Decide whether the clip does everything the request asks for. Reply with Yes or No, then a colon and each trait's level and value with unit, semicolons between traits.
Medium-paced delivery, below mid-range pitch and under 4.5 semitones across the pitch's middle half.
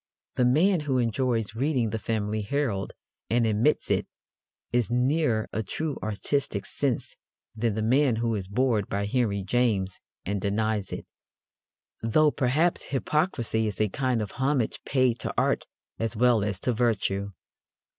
Yes: average, 150 wpm; low, 115 Hz; average, 3.7 semitones